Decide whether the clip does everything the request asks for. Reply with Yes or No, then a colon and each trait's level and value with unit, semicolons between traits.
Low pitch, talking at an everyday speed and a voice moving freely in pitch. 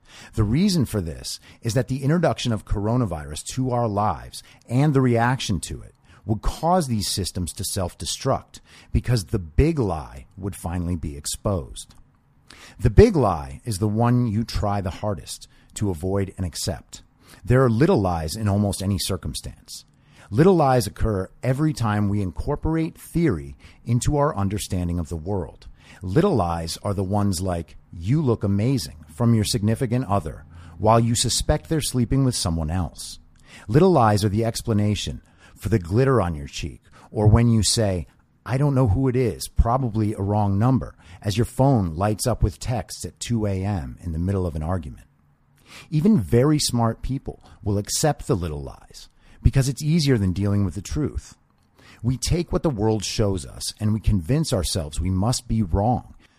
Yes: low, 105 Hz; average, 175 wpm; wide, 5.7 semitones